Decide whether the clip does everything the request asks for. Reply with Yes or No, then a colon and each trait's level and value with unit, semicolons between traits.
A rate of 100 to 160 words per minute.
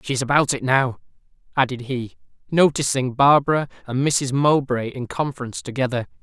Yes: average, 145 wpm